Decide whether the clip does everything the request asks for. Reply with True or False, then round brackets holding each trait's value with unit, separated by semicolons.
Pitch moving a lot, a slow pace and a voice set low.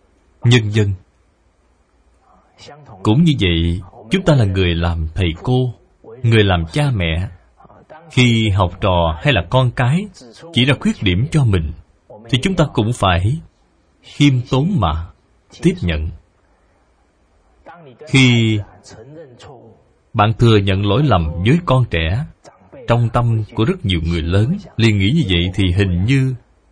True (6.5 semitones; 140 wpm; 105 Hz)